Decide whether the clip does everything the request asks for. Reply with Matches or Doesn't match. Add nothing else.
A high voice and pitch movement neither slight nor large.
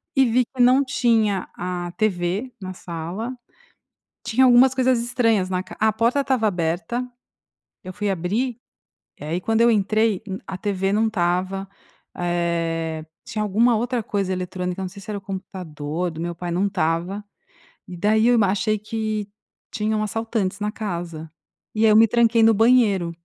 Matches